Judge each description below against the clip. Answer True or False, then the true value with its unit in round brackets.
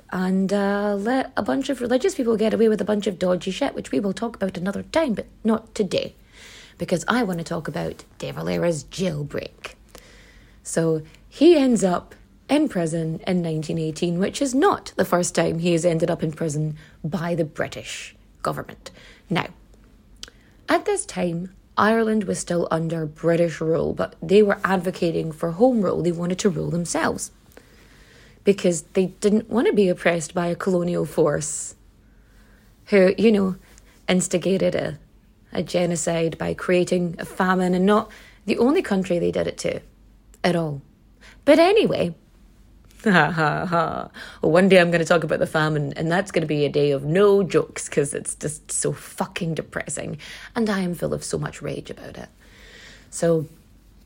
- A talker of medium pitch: True (180 Hz)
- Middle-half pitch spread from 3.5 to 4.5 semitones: True (3.8 semitones)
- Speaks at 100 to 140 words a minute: False (170 wpm)